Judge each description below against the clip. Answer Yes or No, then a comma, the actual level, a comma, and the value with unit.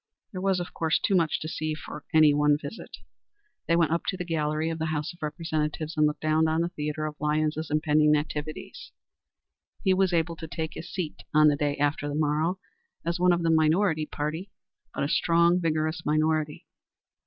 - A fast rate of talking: No, average, 195 wpm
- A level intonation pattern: Yes, narrow, 1.8 semitones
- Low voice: No, medium, 155 Hz